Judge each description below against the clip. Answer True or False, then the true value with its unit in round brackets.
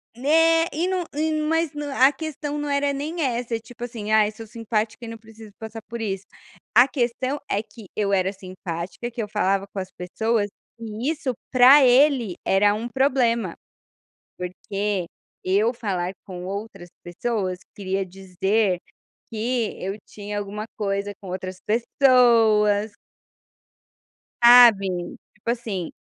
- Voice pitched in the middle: False (220 Hz)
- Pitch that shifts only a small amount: False (4.1 semitones)